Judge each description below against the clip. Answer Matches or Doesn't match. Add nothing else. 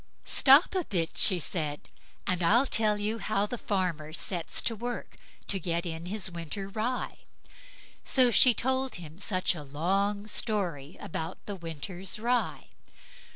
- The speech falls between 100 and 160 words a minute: Matches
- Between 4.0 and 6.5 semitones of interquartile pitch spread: Matches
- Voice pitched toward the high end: Matches